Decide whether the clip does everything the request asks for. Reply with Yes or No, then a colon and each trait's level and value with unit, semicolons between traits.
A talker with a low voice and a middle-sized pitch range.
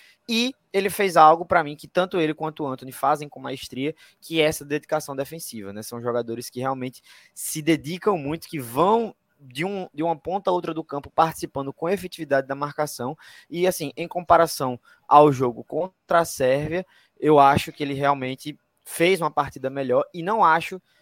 No: medium, 155 Hz; average, 3.9 semitones